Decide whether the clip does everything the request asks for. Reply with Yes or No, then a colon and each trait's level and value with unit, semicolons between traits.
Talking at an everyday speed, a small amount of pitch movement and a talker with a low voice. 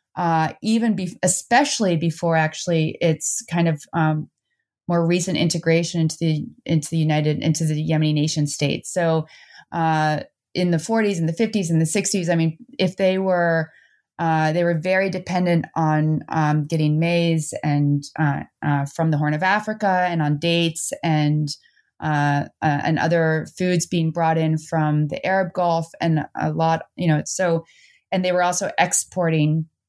No: average, 165 wpm; narrow, 2.3 semitones; medium, 165 Hz